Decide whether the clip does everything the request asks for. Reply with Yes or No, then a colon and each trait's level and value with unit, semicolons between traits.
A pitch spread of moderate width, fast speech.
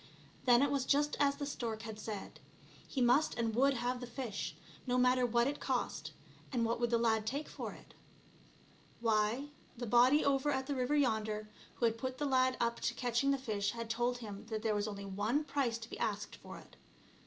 Yes: average, 3.3 semitones; fast, 210 wpm